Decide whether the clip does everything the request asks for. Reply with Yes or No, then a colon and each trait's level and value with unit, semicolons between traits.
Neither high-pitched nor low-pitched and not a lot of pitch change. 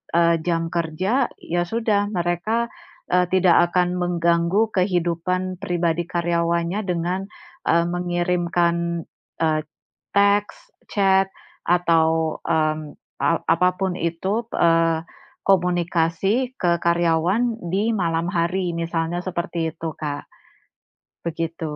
Yes: medium, 175 Hz; narrow, 2.1 semitones